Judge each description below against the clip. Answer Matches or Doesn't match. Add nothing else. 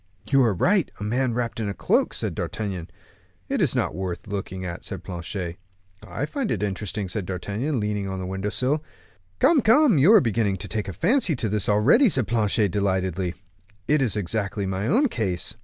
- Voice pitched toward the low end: Matches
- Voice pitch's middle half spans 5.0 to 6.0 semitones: Matches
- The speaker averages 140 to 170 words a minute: Doesn't match